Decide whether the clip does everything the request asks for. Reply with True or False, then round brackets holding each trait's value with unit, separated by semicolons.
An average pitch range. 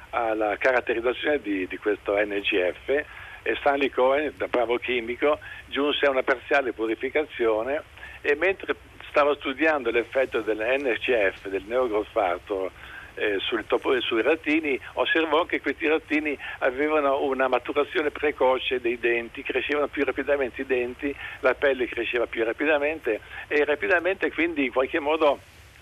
True (4.1 semitones)